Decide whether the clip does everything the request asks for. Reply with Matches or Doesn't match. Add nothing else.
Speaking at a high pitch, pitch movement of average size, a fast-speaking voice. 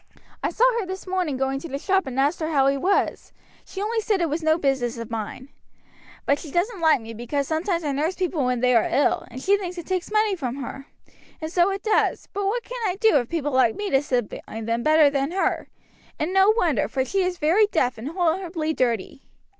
Doesn't match